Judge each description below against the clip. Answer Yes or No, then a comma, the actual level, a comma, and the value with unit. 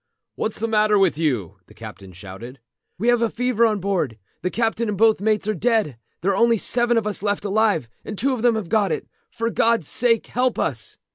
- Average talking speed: No, fast, 220 wpm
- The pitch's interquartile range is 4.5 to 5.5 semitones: Yes, average, 5.2 semitones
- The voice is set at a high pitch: Yes, high, 215 Hz